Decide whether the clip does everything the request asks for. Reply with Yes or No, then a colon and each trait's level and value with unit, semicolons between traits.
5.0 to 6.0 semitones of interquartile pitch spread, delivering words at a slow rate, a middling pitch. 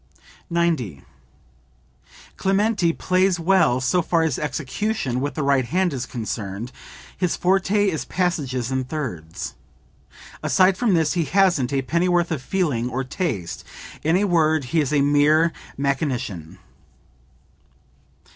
Yes: wide, 5.6 semitones; slow, 130 wpm; medium, 155 Hz